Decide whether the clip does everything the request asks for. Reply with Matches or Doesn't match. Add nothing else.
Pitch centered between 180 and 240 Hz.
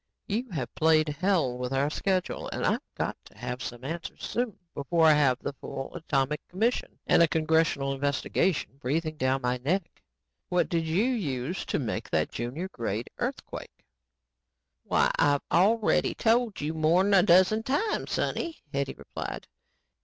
Doesn't match